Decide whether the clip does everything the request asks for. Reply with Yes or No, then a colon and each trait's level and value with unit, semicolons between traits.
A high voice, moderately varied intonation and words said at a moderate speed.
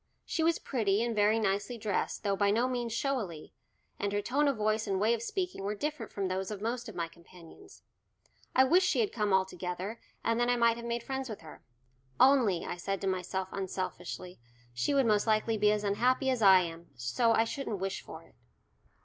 No: high, 215 Hz; average, 4.0 semitones; fast, 210 wpm